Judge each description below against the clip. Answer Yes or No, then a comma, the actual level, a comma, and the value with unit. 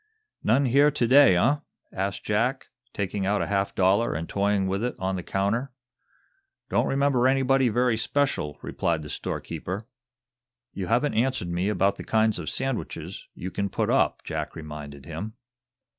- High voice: No, low, 105 Hz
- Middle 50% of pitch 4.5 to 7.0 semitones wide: Yes, average, 5.2 semitones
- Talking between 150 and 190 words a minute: Yes, average, 160 wpm